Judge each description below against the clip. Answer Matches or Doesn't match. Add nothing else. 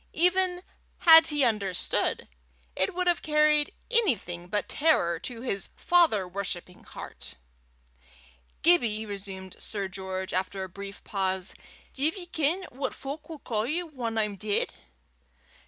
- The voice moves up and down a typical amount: Doesn't match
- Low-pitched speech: Doesn't match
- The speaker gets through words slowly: Matches